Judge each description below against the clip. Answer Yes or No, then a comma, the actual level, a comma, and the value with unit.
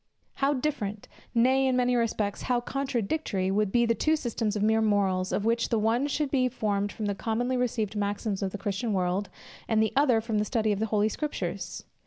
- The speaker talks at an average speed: No, fast, 210 wpm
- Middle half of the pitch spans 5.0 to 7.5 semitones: No, average, 3.4 semitones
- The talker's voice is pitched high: Yes, high, 220 Hz